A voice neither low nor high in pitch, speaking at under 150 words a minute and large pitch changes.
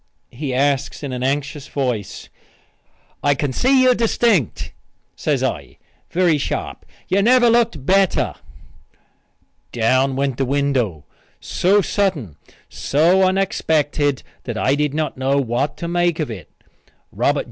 Yes: medium, 145 Hz; slow, 135 wpm; wide, 5.9 semitones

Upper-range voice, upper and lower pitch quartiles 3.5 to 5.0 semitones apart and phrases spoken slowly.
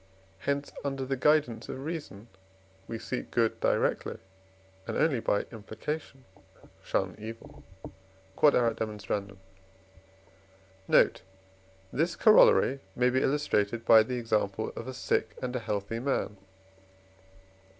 No: low, 120 Hz; average, 4.0 semitones; slow, 110 wpm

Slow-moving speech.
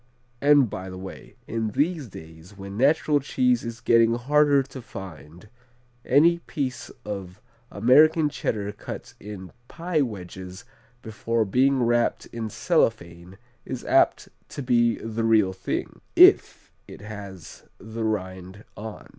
Yes: slow, 130 wpm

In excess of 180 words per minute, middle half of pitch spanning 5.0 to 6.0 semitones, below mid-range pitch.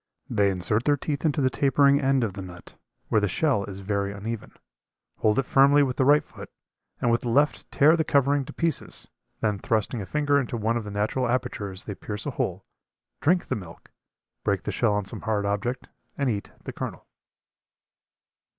Yes: average, 195 wpm; wide, 5.4 semitones; low, 120 Hz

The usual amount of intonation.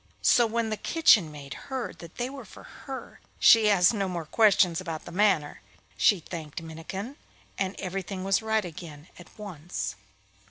Yes: average, 5.0 semitones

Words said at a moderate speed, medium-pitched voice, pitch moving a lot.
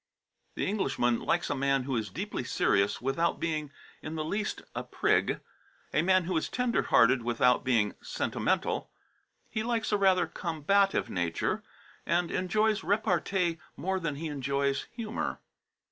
Yes: average, 145 wpm; medium, 165 Hz; wide, 6.3 semitones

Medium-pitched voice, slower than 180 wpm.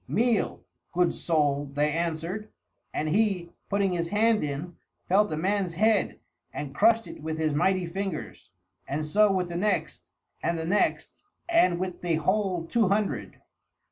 Yes: medium, 180 Hz; average, 155 wpm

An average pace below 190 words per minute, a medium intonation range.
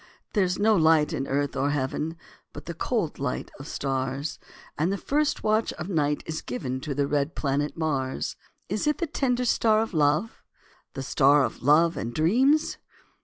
No: average, 180 wpm; wide, 6.4 semitones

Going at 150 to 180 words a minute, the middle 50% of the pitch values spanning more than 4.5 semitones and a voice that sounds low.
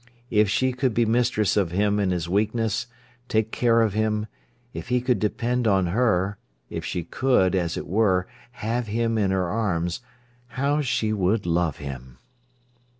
No: average, 165 wpm; average, 4.1 semitones; low, 105 Hz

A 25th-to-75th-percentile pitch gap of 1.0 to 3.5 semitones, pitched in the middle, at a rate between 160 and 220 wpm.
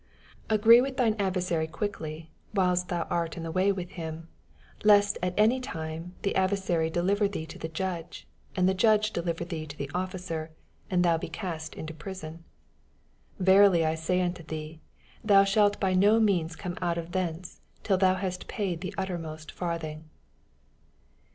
Yes: average, 3.2 semitones; medium, 180 Hz; average, 170 wpm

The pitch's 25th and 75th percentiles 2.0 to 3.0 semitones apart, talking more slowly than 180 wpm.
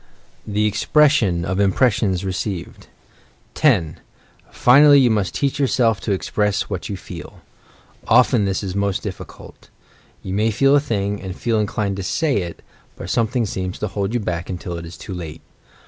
No: average, 4.0 semitones; average, 165 wpm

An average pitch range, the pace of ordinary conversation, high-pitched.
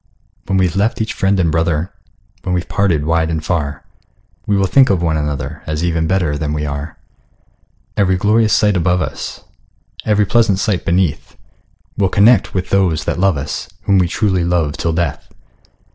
No: average, 3.7 semitones; average, 175 wpm; very low, 90 Hz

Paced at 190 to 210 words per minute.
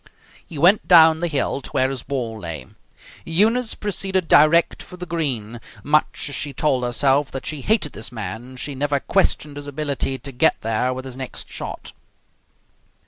No: average, 175 wpm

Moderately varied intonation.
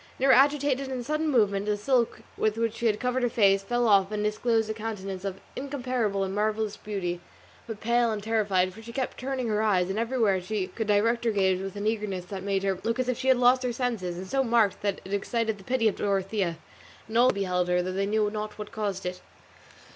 Yes: average, 3.4 semitones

